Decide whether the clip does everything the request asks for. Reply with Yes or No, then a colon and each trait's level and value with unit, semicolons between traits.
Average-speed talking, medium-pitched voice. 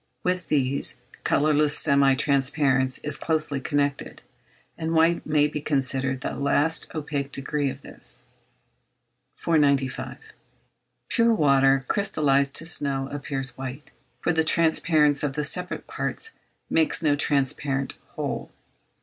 No: slow, 120 wpm; medium, 145 Hz